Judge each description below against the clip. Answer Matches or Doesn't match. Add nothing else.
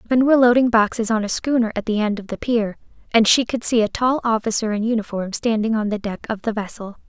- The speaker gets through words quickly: Matches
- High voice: Matches